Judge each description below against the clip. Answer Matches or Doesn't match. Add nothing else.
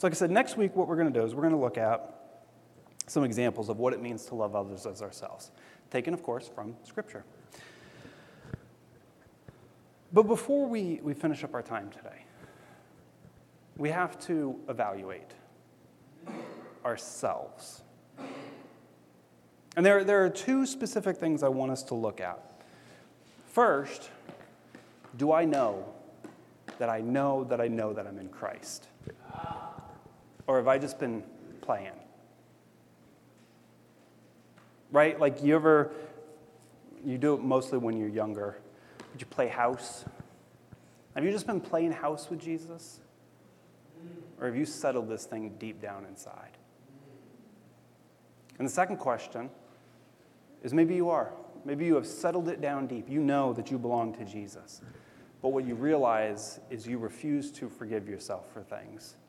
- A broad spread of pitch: Matches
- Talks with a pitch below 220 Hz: Matches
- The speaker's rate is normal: Matches